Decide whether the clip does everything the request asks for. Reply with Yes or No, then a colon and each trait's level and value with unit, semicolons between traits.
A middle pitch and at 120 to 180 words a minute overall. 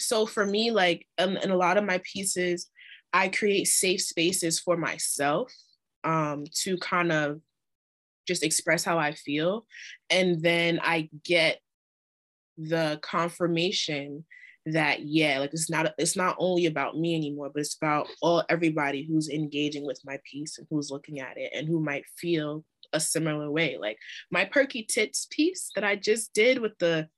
Yes: medium, 165 Hz; average, 170 wpm